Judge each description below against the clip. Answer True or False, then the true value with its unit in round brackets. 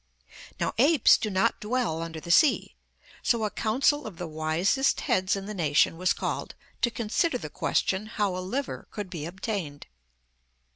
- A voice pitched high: True (195 Hz)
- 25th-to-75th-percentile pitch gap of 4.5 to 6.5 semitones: True (5.3 semitones)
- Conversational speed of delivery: True (165 wpm)